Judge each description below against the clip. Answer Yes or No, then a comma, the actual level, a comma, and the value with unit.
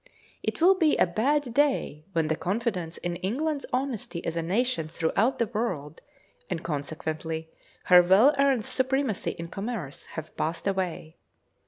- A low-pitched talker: No, high, 190 Hz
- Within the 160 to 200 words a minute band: No, average, 150 wpm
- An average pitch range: No, wide, 7.8 semitones